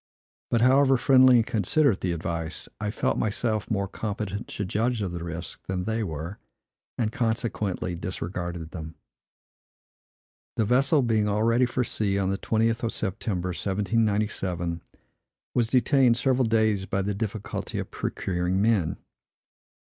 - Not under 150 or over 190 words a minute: No, average, 140 wpm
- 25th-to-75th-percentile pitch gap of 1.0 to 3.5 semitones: No, average, 4.0 semitones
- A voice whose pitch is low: Yes, low, 105 Hz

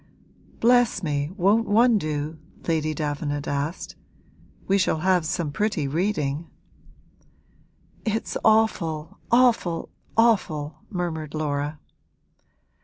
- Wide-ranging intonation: Yes, wide, 5.8 semitones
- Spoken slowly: Yes, slow, 95 wpm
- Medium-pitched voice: Yes, medium, 165 Hz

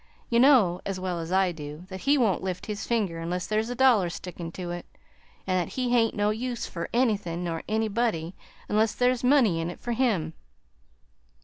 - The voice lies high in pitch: Yes, high, 200 Hz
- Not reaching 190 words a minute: No, average, 195 wpm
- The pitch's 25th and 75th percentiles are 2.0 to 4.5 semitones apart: No, average, 5.2 semitones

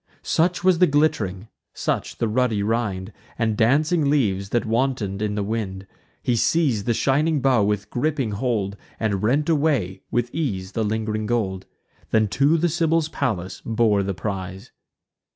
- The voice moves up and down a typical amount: No, wide, 5.8 semitones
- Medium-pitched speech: No, low, 115 Hz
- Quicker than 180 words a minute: No, average, 155 wpm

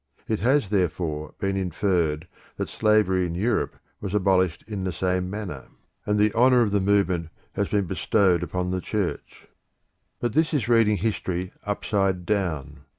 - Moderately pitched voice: No, very low, 95 Hz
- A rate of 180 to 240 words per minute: No, average, 155 wpm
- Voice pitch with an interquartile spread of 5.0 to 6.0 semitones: No, average, 2.8 semitones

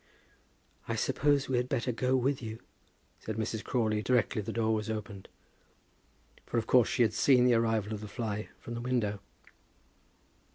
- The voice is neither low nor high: No, low, 115 Hz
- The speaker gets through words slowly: No, average, 170 wpm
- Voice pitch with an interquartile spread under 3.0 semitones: Yes, narrow, 2.5 semitones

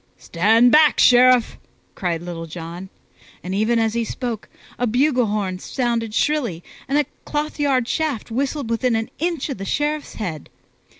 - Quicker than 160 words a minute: No, average, 155 wpm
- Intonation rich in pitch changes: Yes, wide, 5.7 semitones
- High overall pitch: Yes, high, 235 Hz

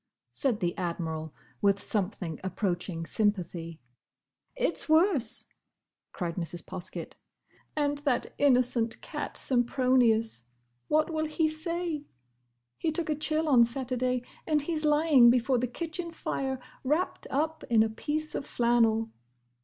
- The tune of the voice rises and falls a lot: Yes, wide, 7.1 semitones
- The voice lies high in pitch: Yes, very high, 250 Hz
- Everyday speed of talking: No, slow, 120 wpm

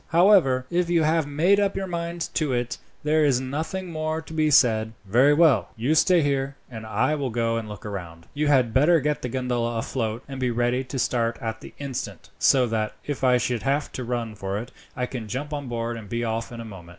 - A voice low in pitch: Yes, low, 130 Hz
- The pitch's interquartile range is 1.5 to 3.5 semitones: No, average, 4.8 semitones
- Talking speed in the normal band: No, fast, 230 wpm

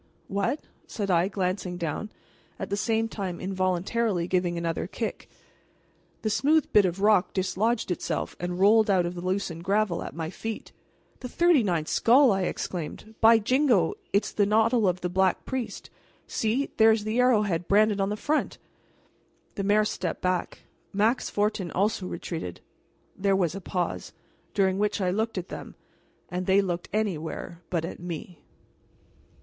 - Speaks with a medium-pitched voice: No, high, 195 Hz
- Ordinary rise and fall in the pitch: Yes, average, 3.4 semitones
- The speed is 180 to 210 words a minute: No, average, 160 wpm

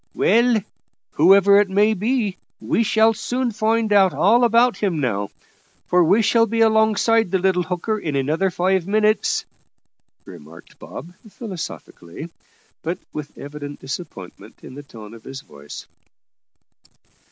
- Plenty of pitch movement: Yes, wide, 6.6 semitones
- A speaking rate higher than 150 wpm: No, slow, 135 wpm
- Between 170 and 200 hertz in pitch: Yes, high, 190 Hz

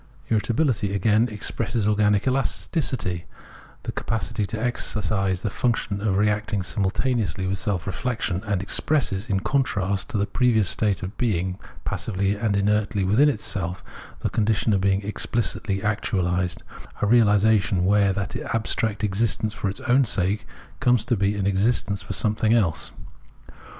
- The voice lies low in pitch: Yes, low, 105 Hz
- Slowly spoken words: No, average, 145 wpm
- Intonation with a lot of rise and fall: No, narrow, 2.5 semitones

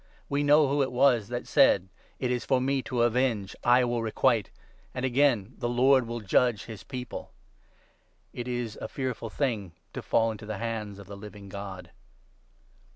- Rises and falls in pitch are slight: No, average, 3.3 semitones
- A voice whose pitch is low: Yes, low, 120 Hz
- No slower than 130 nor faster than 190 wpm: No, fast, 205 wpm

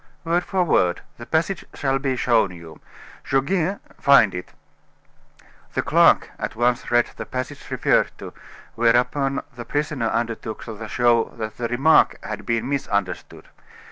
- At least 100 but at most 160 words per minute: Yes, average, 140 wpm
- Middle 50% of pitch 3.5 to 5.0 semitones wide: Yes, average, 3.9 semitones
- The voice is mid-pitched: No, low, 120 Hz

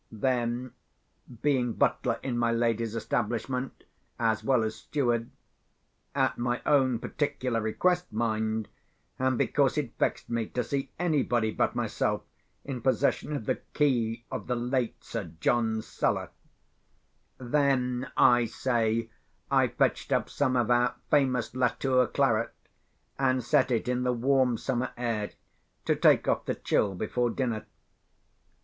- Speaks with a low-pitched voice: Yes, low, 120 Hz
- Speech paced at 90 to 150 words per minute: Yes, slow, 135 wpm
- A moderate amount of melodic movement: No, narrow, 2.3 semitones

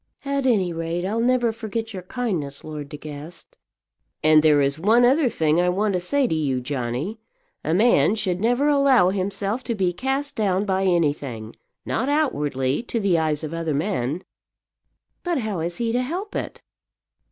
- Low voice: No, medium, 185 Hz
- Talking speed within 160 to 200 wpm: Yes, average, 175 wpm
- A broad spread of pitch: Yes, wide, 7.1 semitones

